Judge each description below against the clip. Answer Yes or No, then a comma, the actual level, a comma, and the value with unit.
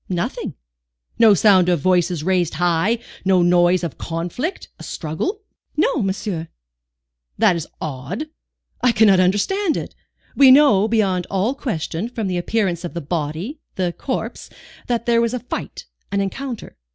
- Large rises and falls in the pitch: No, average, 5.0 semitones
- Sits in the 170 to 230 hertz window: Yes, high, 190 Hz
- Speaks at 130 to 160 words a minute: Yes, average, 150 wpm